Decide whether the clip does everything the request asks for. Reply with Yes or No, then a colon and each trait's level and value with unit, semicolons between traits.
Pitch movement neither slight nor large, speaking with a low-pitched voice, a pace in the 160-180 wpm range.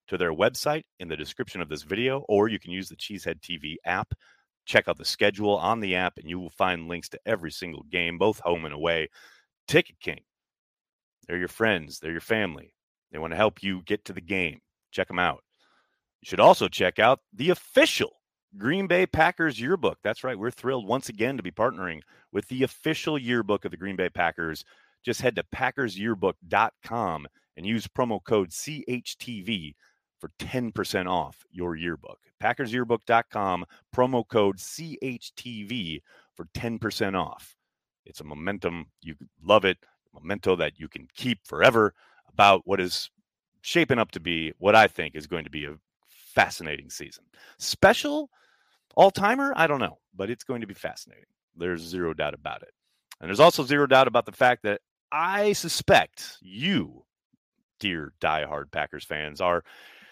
No: wide, 7.0 semitones; low, 105 Hz; average, 170 wpm